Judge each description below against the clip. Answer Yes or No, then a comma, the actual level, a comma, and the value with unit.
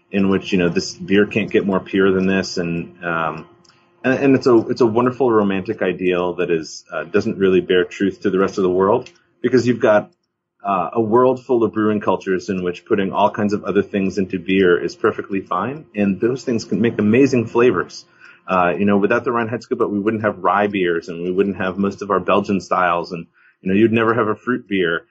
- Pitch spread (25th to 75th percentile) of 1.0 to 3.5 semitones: Yes, average, 3.2 semitones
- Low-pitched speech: Yes, low, 100 Hz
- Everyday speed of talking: No, fast, 230 wpm